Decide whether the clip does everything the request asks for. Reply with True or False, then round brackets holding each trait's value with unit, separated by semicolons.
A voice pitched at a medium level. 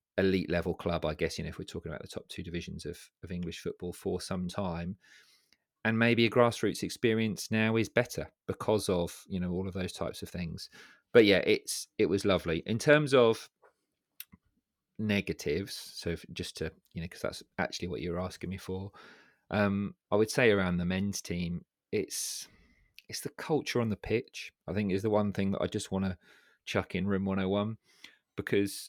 False (95 Hz)